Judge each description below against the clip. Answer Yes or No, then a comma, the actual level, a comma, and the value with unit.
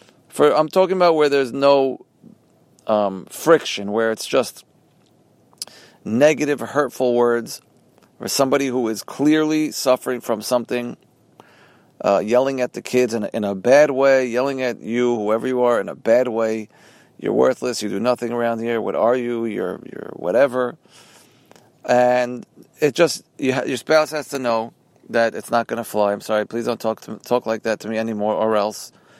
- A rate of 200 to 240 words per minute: No, average, 180 wpm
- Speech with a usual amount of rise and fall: Yes, average, 3.2 semitones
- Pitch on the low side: Yes, low, 120 Hz